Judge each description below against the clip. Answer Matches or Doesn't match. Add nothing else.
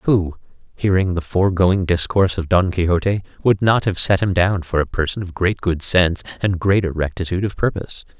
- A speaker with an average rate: Matches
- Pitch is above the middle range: Doesn't match